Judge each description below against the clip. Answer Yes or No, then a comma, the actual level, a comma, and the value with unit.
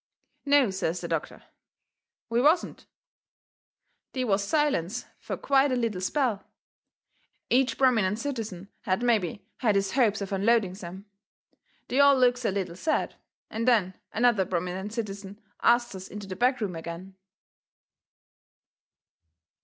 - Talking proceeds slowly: Yes, slow, 130 wpm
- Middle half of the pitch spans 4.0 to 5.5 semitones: Yes, average, 4.7 semitones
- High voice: Yes, high, 210 Hz